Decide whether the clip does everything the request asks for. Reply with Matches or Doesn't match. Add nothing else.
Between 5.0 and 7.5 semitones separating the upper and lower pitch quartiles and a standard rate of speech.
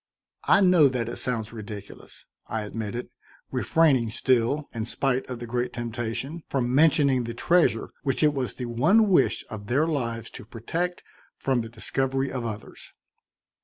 Doesn't match